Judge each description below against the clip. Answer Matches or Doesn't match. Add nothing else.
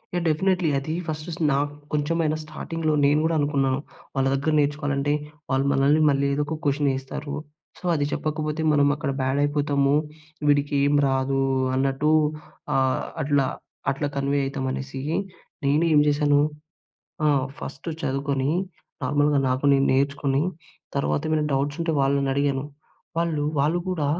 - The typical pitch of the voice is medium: Matches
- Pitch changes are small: Matches